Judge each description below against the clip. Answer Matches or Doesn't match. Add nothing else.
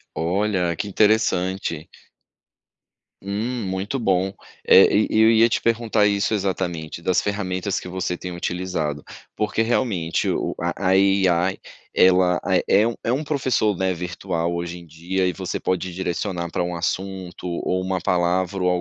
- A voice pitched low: Matches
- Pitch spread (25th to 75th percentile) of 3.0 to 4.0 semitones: Doesn't match